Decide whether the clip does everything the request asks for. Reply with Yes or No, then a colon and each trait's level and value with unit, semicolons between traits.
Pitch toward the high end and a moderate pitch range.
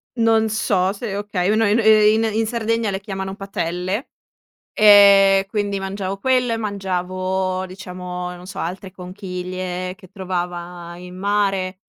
No: high, 195 Hz; narrow, 2.3 semitones